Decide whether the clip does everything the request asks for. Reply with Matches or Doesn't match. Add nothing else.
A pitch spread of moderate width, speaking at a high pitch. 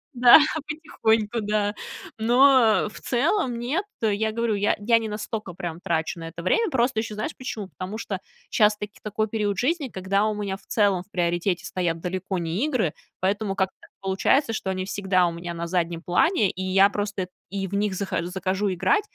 Matches